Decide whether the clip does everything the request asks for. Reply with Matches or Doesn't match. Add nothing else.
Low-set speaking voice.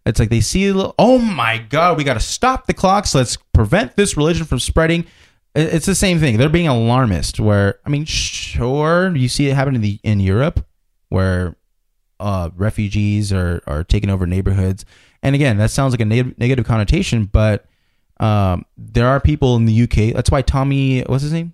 Matches